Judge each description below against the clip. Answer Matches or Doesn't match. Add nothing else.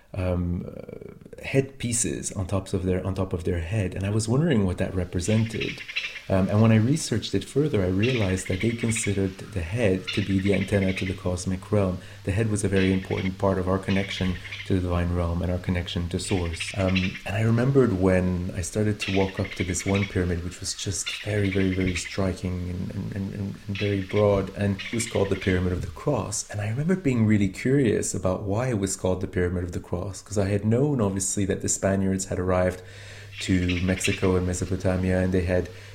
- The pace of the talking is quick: Matches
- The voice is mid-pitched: Doesn't match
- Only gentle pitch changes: Matches